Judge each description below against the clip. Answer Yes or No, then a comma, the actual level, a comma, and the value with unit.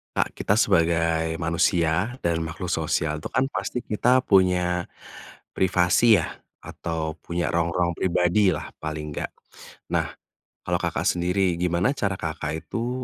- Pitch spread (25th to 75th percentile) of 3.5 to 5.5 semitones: No, average, 2.8 semitones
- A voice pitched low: Yes, very low, 90 Hz